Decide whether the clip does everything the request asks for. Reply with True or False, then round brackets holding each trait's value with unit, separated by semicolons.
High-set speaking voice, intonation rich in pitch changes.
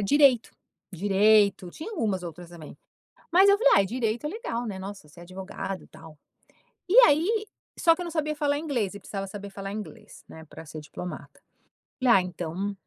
True (205 Hz; 7.8 semitones)